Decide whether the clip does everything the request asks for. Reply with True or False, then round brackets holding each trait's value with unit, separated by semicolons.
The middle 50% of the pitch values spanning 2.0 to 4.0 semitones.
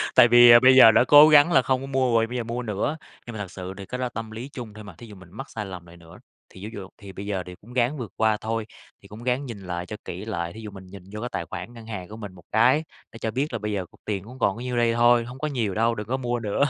True (3.7 semitones)